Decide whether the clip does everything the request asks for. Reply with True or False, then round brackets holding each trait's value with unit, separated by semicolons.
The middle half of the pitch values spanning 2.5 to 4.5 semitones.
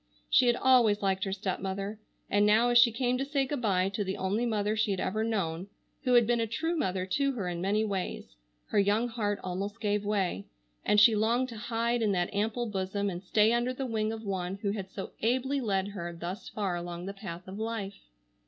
True (3.3 semitones)